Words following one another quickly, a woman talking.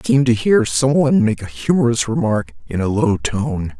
No: fast, 220 wpm; male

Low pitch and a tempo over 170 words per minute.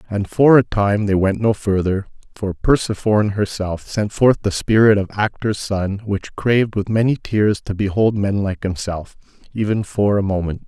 Yes: low, 105 Hz; average, 180 wpm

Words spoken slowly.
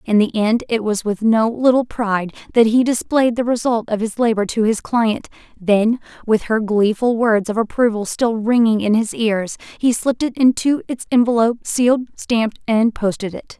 No: average, 190 wpm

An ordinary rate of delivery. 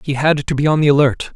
No: fast, 310 wpm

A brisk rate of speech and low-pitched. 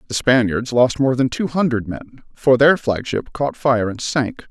Yes: fast, 215 wpm; low, 130 Hz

